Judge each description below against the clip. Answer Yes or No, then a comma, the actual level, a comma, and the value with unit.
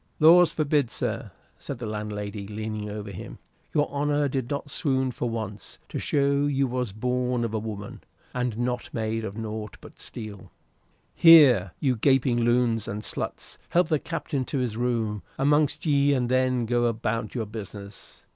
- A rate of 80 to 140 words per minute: No, average, 165 wpm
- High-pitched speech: No, low, 120 Hz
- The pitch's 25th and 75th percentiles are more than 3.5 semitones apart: Yes, average, 4.4 semitones